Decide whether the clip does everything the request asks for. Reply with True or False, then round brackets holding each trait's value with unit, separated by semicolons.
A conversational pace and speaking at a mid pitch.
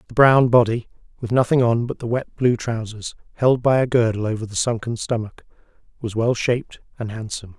False (190 wpm; 115 Hz)